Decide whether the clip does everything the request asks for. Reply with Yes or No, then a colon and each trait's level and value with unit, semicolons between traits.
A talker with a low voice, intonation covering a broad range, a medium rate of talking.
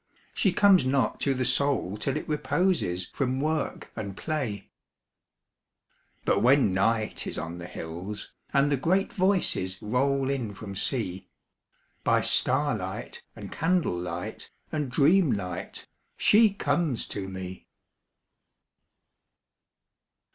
No: low, 130 Hz; wide, 7.9 semitones; slow, 115 wpm